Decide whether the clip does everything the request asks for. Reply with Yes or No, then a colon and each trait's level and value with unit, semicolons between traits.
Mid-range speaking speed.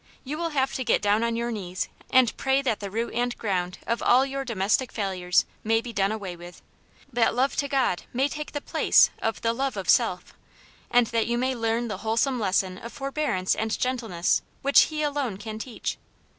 No: fast, 210 wpm